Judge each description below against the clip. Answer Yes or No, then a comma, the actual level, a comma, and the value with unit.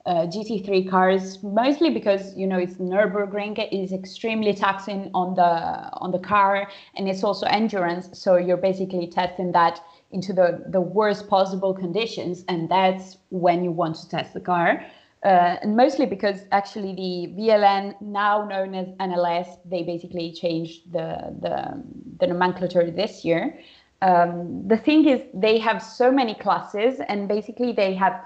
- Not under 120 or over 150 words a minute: No, average, 160 wpm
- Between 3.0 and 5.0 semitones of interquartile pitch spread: No, narrow, 2.6 semitones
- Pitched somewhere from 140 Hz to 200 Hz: Yes, high, 190 Hz